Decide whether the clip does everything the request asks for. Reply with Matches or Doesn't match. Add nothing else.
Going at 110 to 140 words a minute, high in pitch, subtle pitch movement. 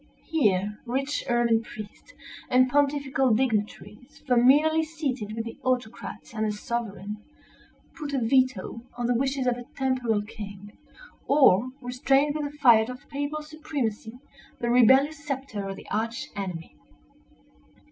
Doesn't match